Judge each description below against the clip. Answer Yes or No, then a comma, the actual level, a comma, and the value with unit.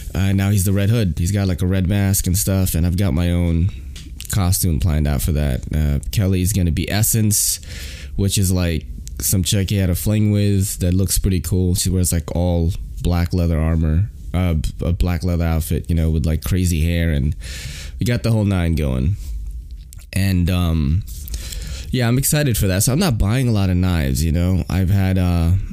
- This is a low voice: Yes, very low, 90 Hz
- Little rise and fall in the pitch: No, average, 3.6 semitones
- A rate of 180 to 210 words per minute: Yes, fast, 205 wpm